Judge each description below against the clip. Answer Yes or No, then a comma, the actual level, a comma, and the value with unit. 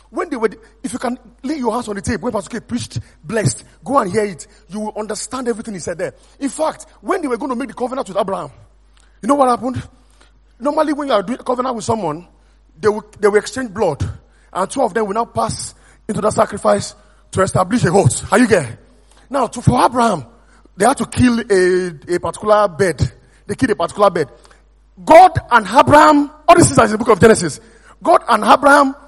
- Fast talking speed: Yes, fast, 220 wpm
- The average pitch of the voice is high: Yes, high, 225 Hz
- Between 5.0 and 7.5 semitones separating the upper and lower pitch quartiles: No, average, 4.5 semitones